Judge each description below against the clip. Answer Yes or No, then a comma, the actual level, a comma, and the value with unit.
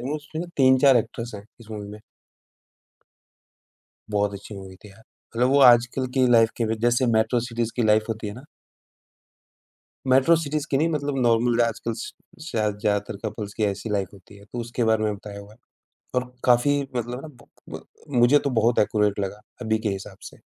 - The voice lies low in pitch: Yes, low, 115 Hz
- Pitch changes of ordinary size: Yes, average, 3.4 semitones